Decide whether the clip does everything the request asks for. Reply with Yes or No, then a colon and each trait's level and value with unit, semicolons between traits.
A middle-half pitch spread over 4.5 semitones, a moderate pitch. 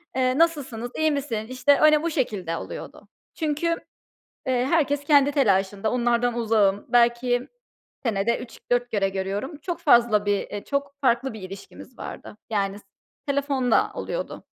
No: average, 5.0 semitones; high, 245 Hz